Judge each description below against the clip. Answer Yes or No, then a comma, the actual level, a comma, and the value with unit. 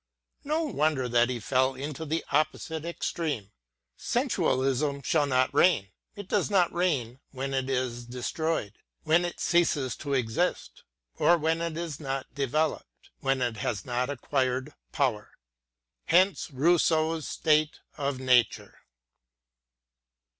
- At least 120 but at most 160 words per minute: Yes, average, 140 wpm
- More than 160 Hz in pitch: No, medium, 140 Hz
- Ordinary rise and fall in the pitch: Yes, average, 4.1 semitones